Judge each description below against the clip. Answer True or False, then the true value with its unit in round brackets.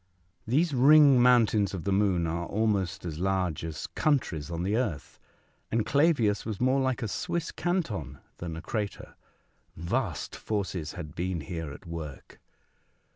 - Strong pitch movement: True (6.8 semitones)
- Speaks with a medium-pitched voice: False (100 Hz)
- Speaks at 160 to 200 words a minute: False (150 wpm)